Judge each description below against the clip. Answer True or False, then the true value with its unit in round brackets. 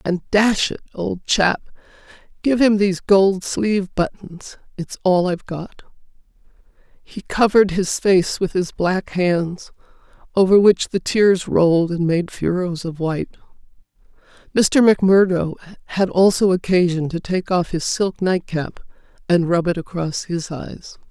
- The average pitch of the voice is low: False (185 Hz)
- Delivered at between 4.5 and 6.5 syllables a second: False (4.2 syllables/s)